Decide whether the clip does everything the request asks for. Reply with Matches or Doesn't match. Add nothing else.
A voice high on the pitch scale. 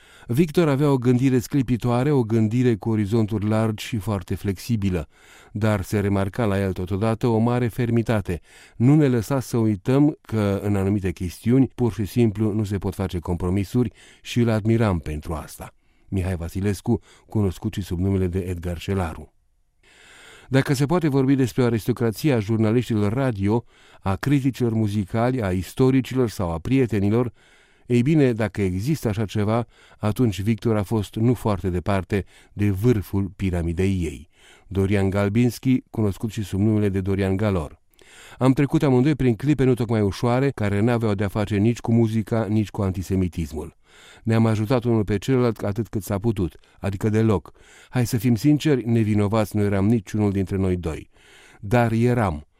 Doesn't match